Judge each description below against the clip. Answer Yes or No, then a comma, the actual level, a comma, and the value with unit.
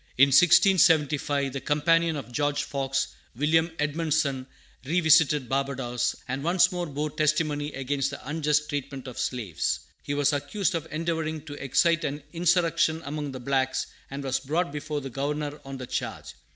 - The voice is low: No, medium, 145 Hz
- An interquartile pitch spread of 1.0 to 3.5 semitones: Yes, average, 2.7 semitones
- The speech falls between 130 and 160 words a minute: Yes, average, 155 wpm